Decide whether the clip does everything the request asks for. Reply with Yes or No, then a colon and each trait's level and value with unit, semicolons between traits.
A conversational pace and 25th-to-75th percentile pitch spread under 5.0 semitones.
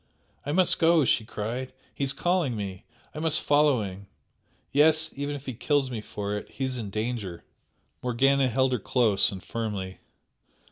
No: average, 175 wpm; average, 5.3 semitones